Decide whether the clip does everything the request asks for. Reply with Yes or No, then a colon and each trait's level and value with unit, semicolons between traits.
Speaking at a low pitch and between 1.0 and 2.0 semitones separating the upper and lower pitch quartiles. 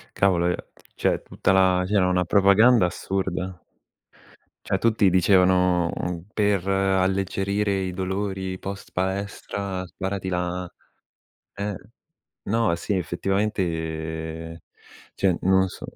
Yes: very low, 95 Hz; narrow, 1.6 semitones